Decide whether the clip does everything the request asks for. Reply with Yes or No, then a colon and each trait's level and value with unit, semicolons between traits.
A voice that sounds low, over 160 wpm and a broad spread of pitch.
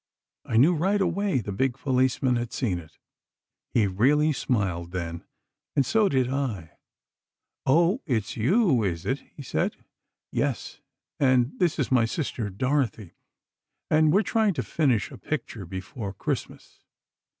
No: low, 130 Hz; average, 140 wpm; wide, 6.8 semitones